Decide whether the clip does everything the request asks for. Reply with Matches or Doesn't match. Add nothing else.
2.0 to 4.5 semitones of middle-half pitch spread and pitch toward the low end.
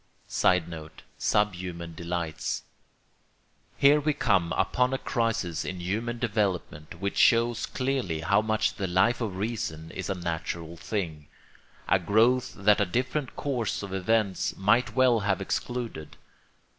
Doesn't match